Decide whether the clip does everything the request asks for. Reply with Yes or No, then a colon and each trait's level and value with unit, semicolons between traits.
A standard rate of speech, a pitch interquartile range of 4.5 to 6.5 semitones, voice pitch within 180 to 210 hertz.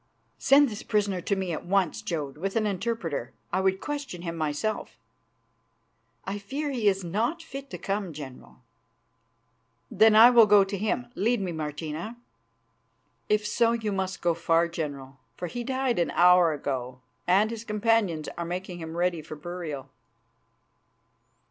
Yes: average, 155 wpm; average, 4.9 semitones; high, 190 Hz